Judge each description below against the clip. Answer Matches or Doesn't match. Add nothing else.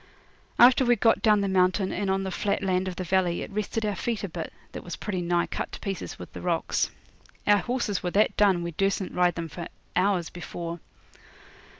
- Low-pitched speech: Doesn't match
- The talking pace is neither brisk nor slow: Doesn't match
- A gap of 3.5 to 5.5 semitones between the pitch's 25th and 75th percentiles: Doesn't match